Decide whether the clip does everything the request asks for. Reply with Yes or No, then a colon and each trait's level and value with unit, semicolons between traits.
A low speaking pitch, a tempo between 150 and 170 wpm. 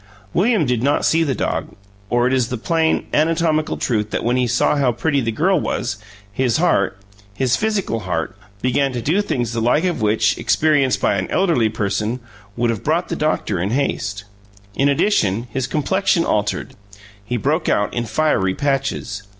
No: low, 130 Hz; average, 180 wpm